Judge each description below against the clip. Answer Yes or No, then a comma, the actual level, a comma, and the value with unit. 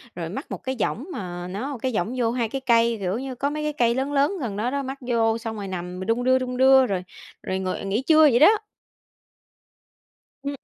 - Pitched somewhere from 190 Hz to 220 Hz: No, high, 240 Hz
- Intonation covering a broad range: No, average, 4.7 semitones